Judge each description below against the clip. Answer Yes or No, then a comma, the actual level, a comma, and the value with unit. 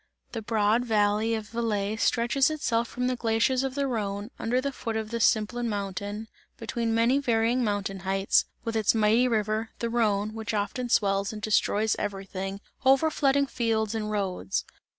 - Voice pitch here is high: Yes, high, 220 Hz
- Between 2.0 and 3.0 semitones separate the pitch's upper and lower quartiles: Yes, narrow, 2.5 semitones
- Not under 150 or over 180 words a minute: Yes, average, 165 wpm